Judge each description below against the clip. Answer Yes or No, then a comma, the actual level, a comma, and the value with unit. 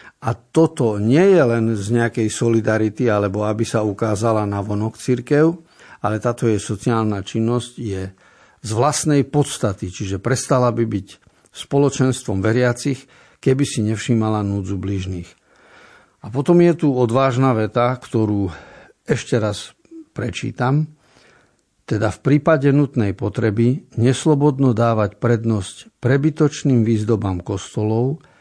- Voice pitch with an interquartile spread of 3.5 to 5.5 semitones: Yes, average, 4.0 semitones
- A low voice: Yes, low, 120 Hz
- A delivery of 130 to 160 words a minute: No, average, 120 wpm